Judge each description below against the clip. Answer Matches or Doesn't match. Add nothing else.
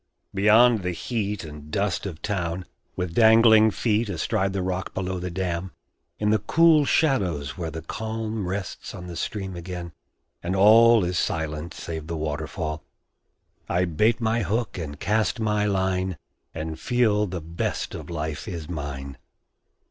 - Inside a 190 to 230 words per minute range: Doesn't match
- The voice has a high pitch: Doesn't match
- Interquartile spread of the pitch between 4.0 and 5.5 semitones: Matches